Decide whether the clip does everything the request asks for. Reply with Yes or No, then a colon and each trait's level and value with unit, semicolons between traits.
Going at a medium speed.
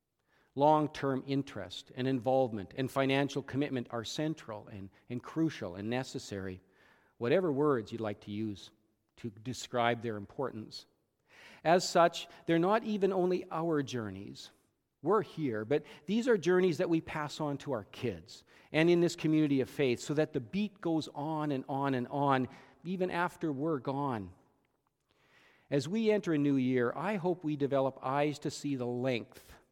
Yes: average, 165 wpm